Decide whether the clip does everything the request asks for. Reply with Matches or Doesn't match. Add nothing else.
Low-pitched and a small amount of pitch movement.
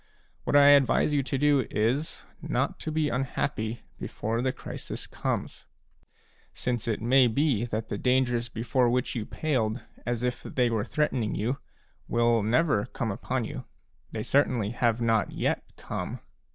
Doesn't match